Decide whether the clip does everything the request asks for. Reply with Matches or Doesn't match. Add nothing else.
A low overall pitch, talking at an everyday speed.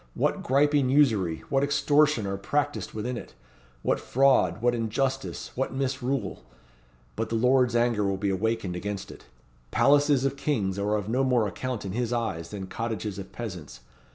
Matches